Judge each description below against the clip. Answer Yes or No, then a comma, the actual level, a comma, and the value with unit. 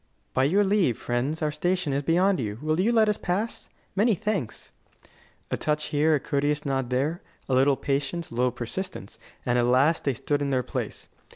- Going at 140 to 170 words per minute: No, average, 195 wpm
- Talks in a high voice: No, medium, 150 Hz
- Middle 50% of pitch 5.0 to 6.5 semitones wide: Yes, wide, 5.4 semitones